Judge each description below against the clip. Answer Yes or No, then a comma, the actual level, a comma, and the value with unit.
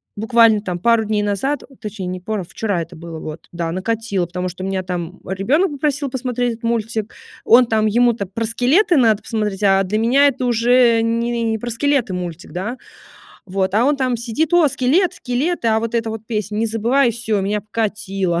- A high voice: Yes, high, 225 Hz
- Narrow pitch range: No, average, 3.8 semitones